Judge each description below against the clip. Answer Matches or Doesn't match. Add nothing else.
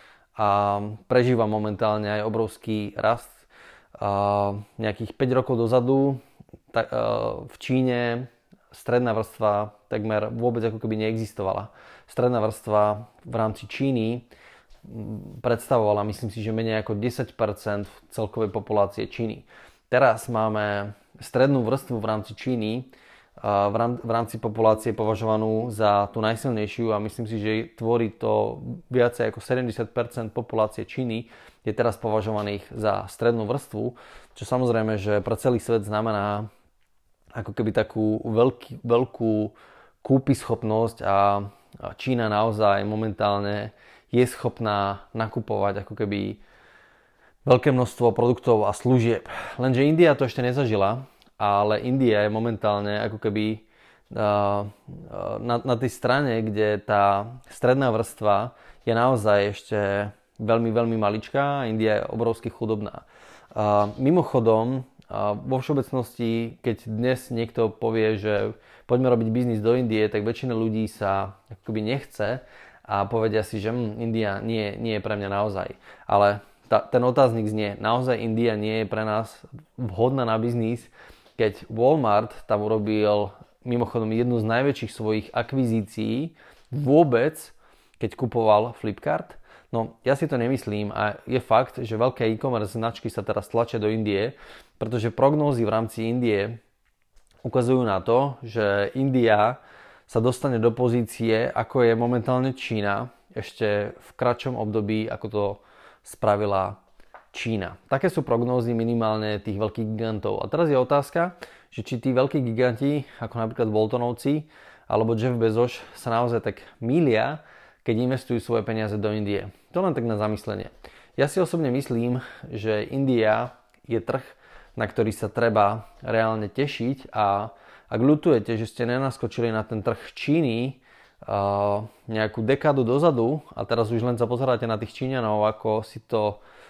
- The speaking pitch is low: Matches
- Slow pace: Doesn't match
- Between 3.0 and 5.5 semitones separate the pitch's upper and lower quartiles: Doesn't match